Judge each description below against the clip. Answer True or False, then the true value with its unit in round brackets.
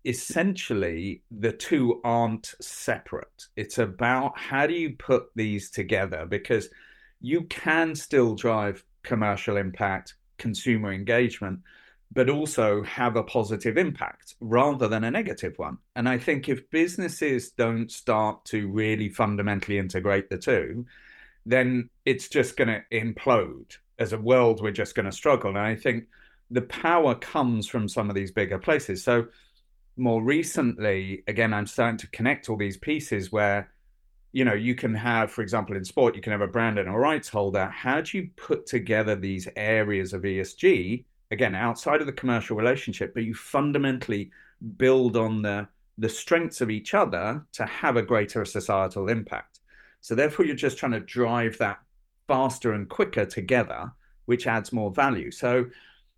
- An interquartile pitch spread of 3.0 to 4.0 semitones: True (3.4 semitones)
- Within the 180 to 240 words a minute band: False (160 wpm)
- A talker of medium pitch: False (115 Hz)